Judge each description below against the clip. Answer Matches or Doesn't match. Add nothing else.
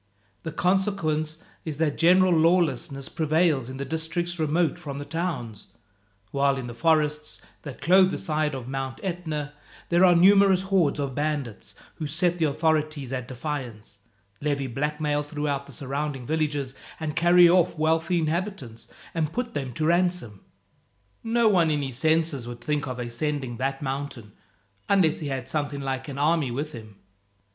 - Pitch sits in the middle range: Matches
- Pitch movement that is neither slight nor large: Matches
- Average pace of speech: Matches